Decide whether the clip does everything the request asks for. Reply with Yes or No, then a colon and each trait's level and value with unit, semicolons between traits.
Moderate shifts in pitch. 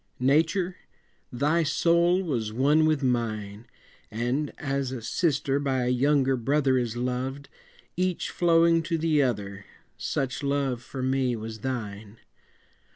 Yes: average, 4.1 semitones